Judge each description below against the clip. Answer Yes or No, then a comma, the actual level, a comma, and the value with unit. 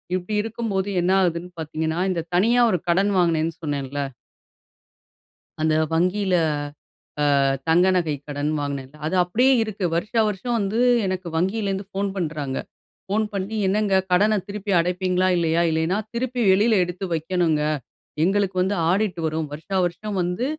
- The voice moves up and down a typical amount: Yes, average, 3.7 semitones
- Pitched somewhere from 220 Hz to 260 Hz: No, medium, 185 Hz